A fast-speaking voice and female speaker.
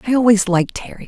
Yes: fast, 225 wpm; female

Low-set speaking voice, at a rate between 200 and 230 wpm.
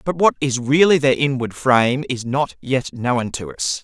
Yes: low, 130 Hz; fast, 205 wpm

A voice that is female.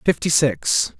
No: male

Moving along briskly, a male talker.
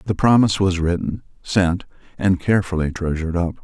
No: average, 150 wpm; male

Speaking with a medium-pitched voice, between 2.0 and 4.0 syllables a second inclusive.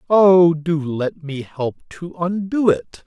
Yes: medium, 160 Hz; 3.3 syllables/s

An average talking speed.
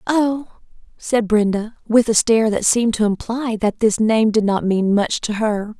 Yes: average, 195 wpm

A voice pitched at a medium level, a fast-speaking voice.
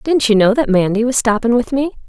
No: high, 240 Hz; fast, 260 wpm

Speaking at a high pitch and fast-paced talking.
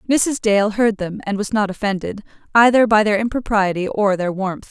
No: high, 210 Hz; average, 190 wpm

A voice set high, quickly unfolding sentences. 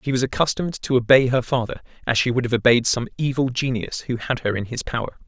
No: low, 125 Hz; fast, 240 wpm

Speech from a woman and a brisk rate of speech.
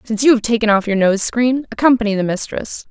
Yes: female; fast, 225 wpm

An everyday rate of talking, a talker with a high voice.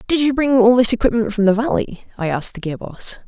No: fast, 255 wpm; high, 225 Hz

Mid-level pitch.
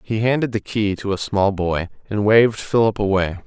No: low, 105 Hz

